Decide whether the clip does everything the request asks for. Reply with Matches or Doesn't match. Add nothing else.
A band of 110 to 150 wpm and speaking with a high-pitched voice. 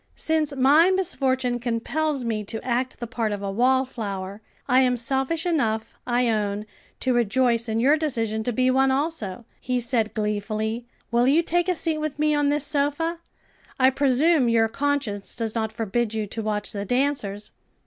Doesn't match